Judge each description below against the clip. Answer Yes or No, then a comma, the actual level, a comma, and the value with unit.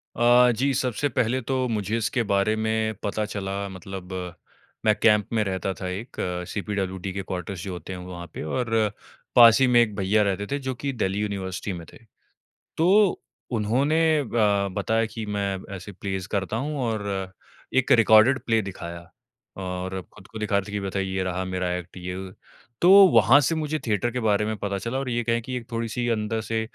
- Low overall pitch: Yes, low, 105 Hz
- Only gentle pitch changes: No, average, 3.4 semitones